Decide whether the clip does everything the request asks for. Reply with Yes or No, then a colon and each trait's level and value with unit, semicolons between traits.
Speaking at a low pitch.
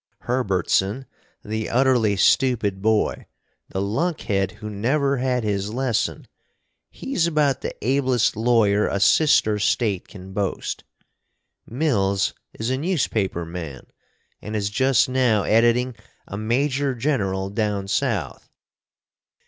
Yes: low, 110 Hz